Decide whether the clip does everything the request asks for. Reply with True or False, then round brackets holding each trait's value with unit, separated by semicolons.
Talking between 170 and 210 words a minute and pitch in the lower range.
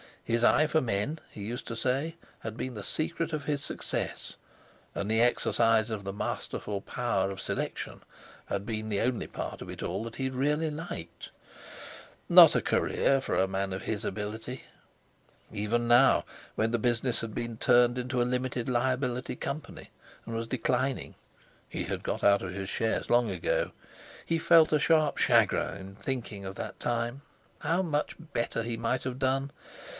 True (175 wpm; 120 Hz)